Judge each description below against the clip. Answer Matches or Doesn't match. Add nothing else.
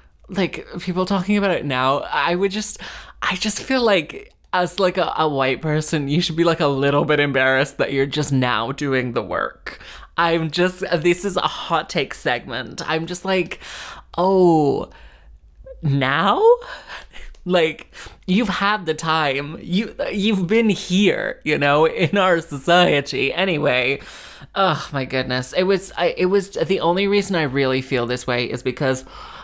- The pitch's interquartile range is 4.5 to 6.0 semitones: Matches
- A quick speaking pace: Doesn't match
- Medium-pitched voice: Matches